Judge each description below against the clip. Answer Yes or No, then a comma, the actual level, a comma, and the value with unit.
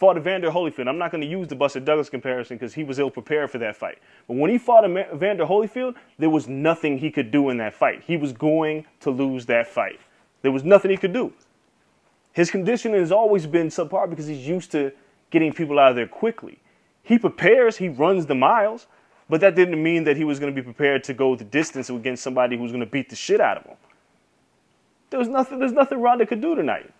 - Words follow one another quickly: Yes, fast, 240 wpm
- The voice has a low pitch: No, medium, 155 Hz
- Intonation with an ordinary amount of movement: No, wide, 6.3 semitones